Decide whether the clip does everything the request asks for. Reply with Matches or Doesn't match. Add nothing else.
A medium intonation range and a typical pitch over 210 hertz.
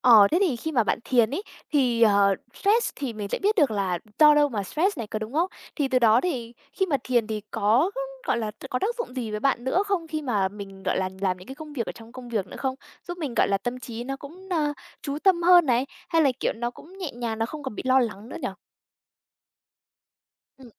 Doesn't match